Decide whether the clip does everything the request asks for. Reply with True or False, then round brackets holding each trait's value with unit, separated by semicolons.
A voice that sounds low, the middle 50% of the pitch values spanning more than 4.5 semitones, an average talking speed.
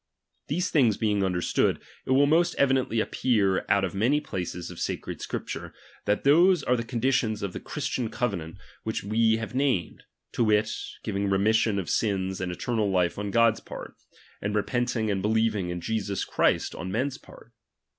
False (110 Hz; 3.9 semitones; 175 wpm)